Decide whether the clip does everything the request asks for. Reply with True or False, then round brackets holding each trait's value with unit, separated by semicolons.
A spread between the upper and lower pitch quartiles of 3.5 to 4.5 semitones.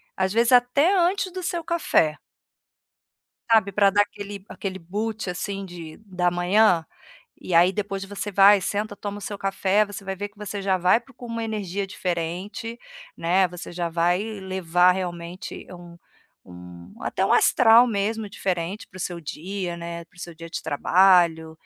False (3.0 semitones)